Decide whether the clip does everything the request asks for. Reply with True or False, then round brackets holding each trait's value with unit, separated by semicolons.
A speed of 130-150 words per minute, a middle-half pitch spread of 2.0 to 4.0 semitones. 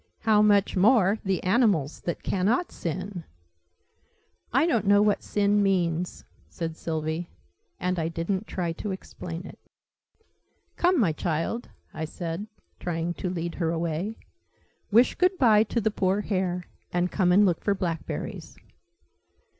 True (140 wpm; 3.7 semitones)